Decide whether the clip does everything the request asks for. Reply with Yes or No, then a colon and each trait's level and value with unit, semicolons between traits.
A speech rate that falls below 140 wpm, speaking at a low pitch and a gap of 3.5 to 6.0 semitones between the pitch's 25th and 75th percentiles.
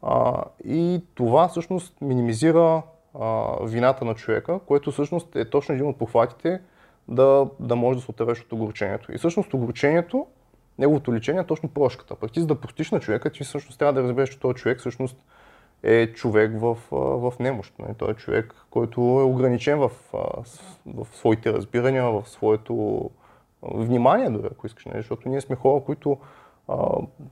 No: average, 160 wpm; low, 130 Hz; average, 3.8 semitones